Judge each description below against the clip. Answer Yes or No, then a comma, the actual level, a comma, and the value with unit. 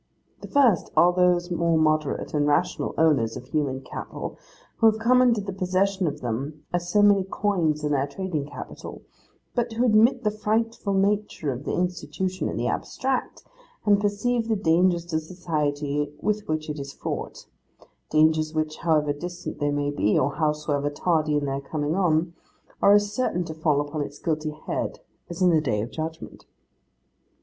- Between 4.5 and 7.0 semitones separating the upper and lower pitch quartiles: Yes, average, 4.9 semitones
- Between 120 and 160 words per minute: No, average, 175 wpm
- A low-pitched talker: No, medium, 160 Hz